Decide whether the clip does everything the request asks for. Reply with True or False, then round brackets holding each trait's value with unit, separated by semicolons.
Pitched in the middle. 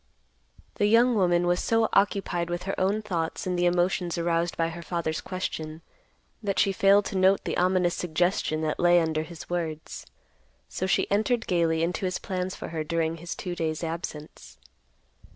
True (175 Hz)